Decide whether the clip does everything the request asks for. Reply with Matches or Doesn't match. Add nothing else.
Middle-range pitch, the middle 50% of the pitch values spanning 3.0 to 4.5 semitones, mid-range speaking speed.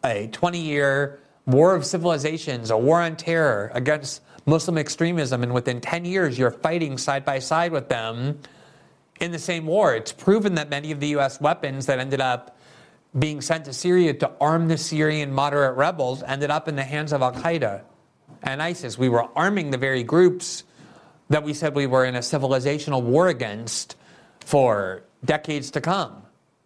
Matches